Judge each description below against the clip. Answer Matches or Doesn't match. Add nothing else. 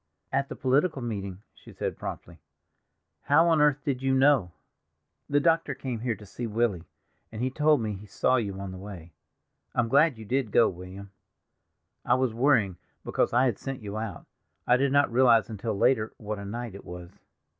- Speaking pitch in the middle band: Doesn't match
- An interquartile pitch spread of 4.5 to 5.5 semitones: Matches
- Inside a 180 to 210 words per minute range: Matches